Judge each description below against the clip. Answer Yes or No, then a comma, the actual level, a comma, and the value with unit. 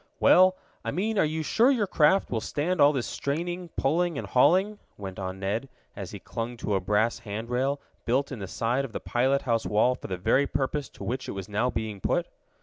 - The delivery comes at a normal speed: No, fast, 225 wpm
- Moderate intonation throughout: No, wide, 6.1 semitones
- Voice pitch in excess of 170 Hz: No, low, 130 Hz